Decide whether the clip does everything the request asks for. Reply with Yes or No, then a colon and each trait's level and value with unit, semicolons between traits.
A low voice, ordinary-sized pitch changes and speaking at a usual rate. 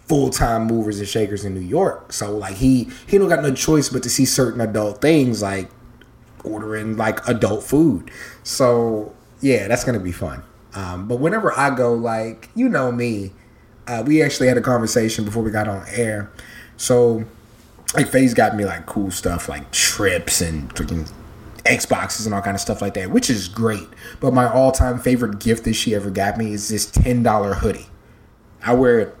Yes: low, 115 Hz; average, 3.4 semitones; average, 190 wpm